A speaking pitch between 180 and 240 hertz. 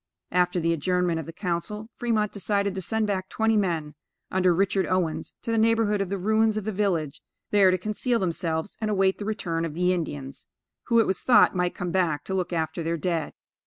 Yes: medium, 185 Hz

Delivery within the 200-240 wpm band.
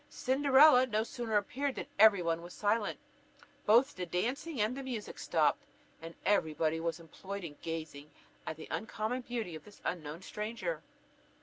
No: average, 165 wpm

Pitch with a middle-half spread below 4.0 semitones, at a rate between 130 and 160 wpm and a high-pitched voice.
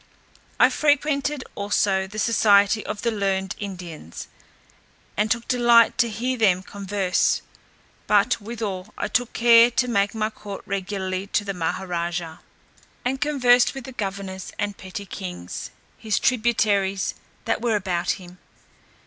Yes: average, 3.6 semitones; average, 140 wpm; high, 205 Hz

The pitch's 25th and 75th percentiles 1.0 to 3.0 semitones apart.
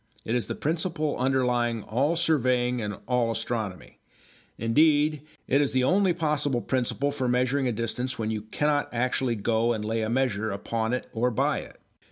No: average, 3.8 semitones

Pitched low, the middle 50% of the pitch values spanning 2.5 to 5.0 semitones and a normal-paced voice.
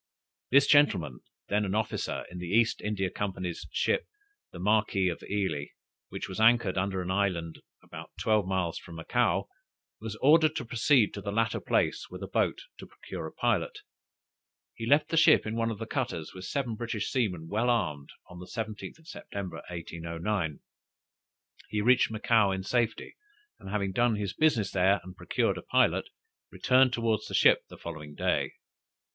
Yes: low, 105 Hz; average, 4.2 semitones; average, 170 wpm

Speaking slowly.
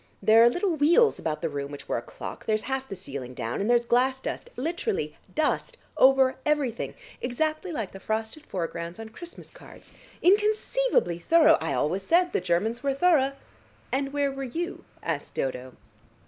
No: average, 175 wpm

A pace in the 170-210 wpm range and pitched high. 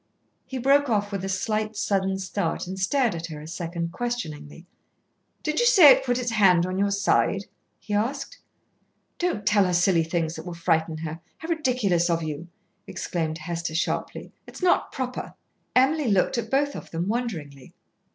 Yes: average, 175 wpm; high, 195 Hz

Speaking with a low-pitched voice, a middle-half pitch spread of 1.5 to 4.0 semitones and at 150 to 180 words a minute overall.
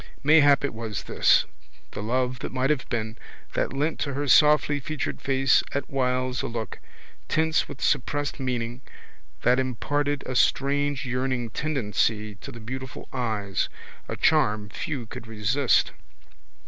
No: low, 130 Hz; average, 3.6 semitones; average, 140 wpm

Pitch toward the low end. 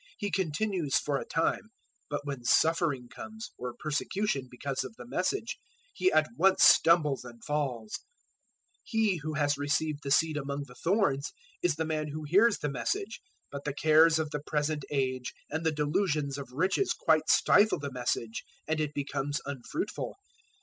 No: medium, 150 Hz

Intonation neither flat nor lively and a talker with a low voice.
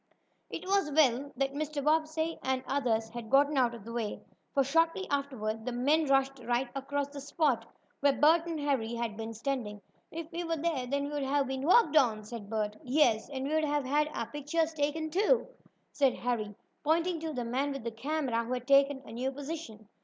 No: average, 4.2 semitones; very high, 275 Hz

